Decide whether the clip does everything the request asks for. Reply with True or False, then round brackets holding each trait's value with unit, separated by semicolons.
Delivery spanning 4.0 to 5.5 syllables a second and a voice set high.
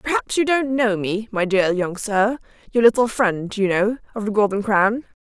True (4.7 syllables/s; 215 Hz)